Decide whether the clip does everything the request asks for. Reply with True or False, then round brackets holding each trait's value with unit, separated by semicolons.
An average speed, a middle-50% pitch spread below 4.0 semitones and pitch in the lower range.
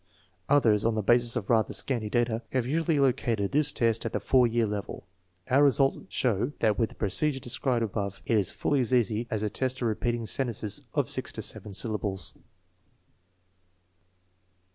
True (180 wpm; 3.3 semitones; 115 Hz)